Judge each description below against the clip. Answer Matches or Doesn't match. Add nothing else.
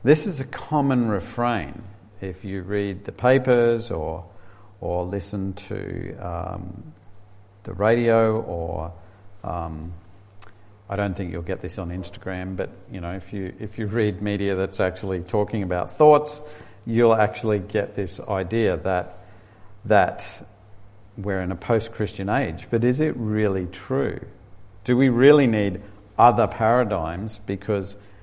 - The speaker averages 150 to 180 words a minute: Doesn't match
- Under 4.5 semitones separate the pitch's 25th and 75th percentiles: Matches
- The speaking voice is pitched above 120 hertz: Doesn't match